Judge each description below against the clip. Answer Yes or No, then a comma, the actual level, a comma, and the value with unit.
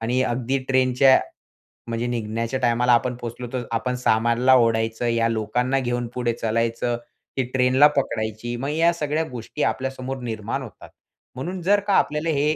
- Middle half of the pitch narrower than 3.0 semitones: Yes, narrow, 2.4 semitones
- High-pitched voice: No, low, 125 Hz